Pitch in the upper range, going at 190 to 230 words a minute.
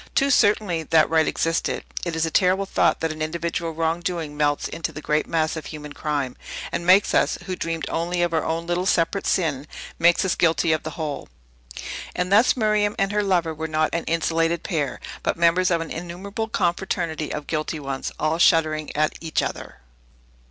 No: medium, 165 Hz; average, 195 wpm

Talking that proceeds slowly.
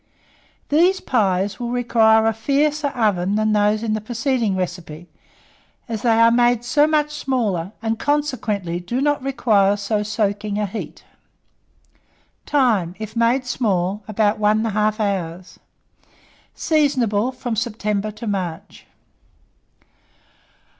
Yes: slow, 120 wpm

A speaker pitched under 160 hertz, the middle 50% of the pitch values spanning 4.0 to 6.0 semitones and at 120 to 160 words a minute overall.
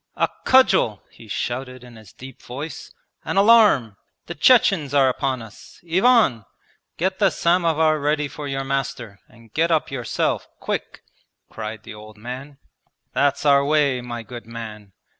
Yes: low, 135 Hz; average, 5.2 semitones; average, 150 wpm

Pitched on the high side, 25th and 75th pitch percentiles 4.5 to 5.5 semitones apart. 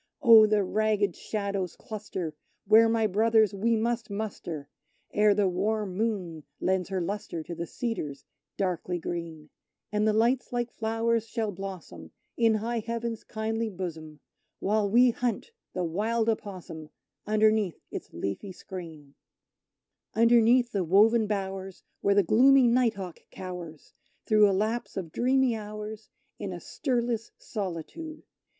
No: high, 210 Hz; average, 3.6 semitones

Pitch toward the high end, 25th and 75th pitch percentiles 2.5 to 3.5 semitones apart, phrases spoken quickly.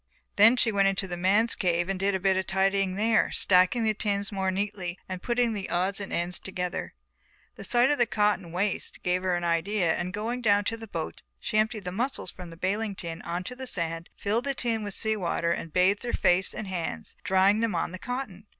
Yes: high, 195 Hz; average, 3.1 semitones; fast, 230 wpm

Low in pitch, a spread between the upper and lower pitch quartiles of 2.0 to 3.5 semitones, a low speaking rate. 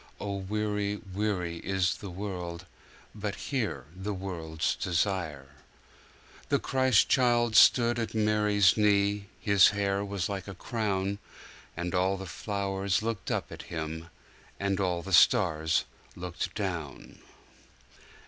Yes: low, 100 Hz; average, 2.9 semitones; slow, 110 wpm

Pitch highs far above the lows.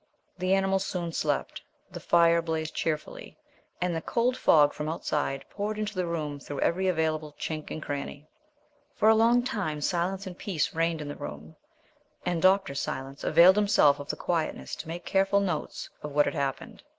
No: average, 4.2 semitones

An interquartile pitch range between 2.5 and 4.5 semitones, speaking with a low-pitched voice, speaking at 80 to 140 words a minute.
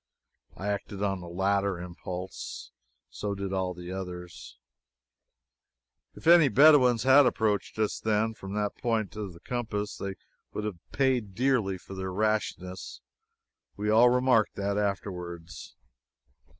Yes: average, 3.1 semitones; low, 100 Hz; slow, 135 wpm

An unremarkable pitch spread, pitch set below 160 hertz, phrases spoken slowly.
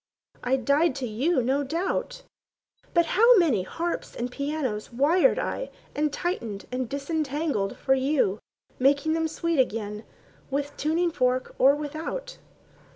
No: average, 4.3 semitones; very high, 285 Hz; slow, 130 wpm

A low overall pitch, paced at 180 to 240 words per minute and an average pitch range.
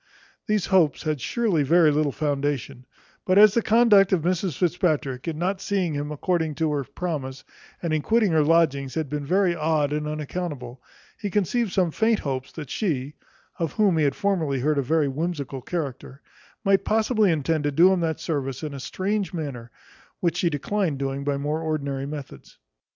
No: medium, 155 Hz; average, 185 wpm; average, 4.6 semitones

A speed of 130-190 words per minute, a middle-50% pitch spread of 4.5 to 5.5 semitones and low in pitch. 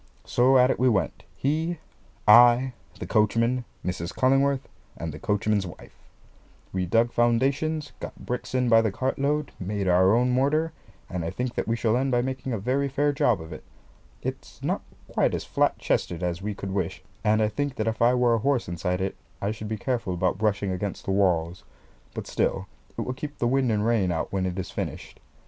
No: fast, 205 wpm; average, 5.2 semitones; low, 115 Hz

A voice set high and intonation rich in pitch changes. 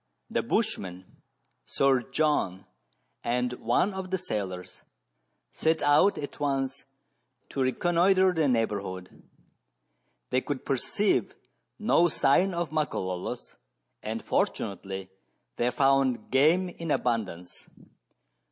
No: low, 135 Hz; wide, 7.9 semitones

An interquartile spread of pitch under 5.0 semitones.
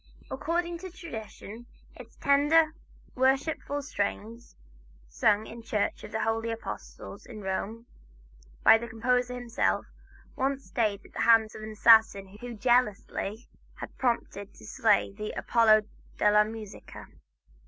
Yes: average, 2.9 semitones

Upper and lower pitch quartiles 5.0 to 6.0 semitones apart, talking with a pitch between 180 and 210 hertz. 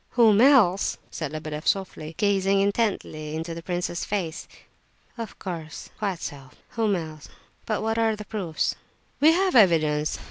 Yes: average, 5.3 semitones; high, 190 Hz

